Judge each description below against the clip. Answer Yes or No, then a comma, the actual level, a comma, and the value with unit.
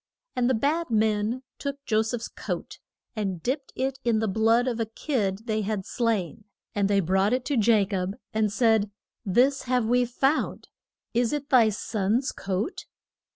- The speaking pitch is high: Yes, high, 225 Hz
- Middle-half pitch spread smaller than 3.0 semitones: No, average, 3.4 semitones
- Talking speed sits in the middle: Yes, average, 170 wpm